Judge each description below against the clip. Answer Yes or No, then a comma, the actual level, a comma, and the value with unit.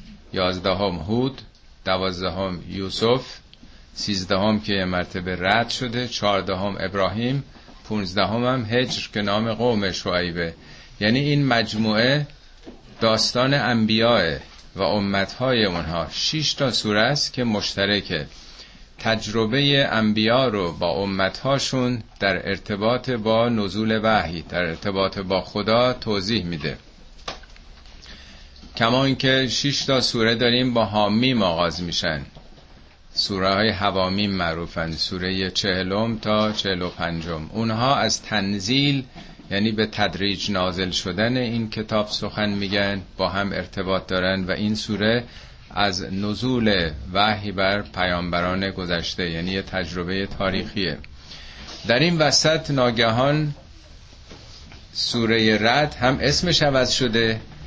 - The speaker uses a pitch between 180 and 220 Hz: No, low, 100 Hz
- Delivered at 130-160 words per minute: No, average, 110 wpm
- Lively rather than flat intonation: No, average, 4.1 semitones